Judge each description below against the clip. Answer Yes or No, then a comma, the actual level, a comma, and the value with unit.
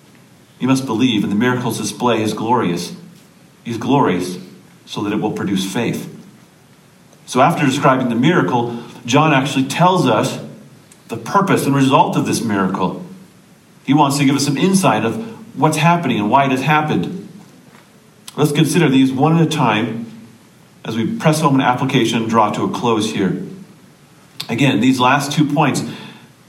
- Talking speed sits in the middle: Yes, average, 165 wpm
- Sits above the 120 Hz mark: Yes, low, 135 Hz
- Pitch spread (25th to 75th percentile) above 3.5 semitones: Yes, average, 4.4 semitones